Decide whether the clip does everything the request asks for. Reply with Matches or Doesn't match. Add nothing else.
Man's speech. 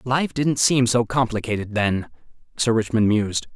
Matches